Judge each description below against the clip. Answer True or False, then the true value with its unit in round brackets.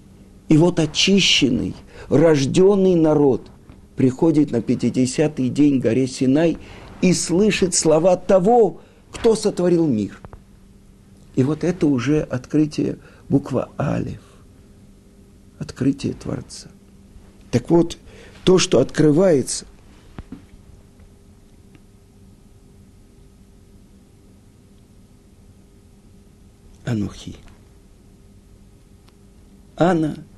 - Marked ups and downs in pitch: True (7.7 semitones)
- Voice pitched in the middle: False (105 Hz)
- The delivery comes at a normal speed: False (70 wpm)